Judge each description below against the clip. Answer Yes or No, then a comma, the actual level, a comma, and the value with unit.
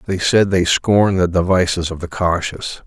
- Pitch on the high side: No, very low, 90 Hz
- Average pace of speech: Yes, average, 190 wpm